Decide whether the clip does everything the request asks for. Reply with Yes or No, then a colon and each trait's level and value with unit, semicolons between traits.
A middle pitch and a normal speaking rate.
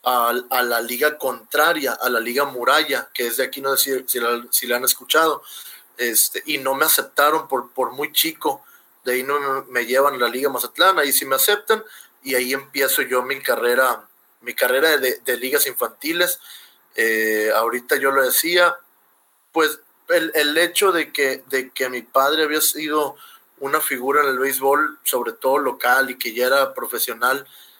Yes: medium, 145 Hz; average, 180 wpm